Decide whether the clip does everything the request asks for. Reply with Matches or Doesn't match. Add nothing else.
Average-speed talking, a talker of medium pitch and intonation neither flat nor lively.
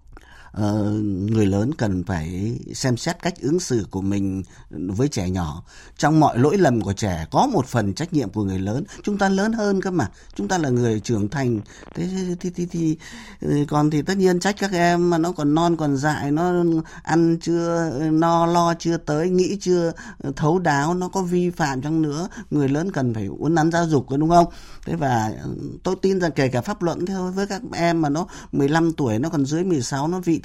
Doesn't match